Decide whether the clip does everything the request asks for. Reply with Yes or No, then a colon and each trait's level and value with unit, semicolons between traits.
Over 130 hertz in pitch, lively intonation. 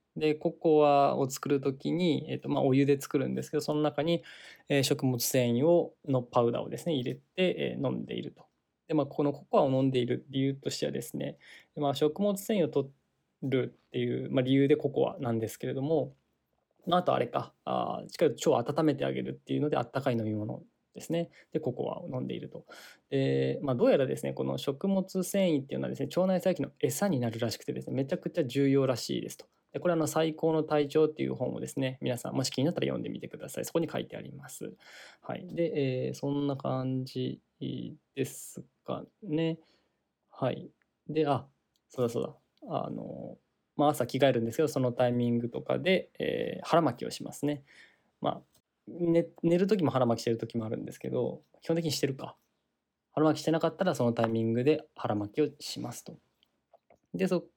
No: medium, 140 Hz; average, 4.0 semitones